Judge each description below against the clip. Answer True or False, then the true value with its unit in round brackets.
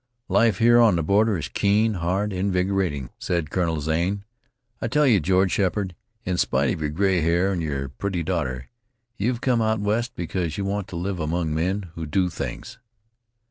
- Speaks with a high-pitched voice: False (90 Hz)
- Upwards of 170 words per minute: True (185 wpm)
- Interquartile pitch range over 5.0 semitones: False (3.7 semitones)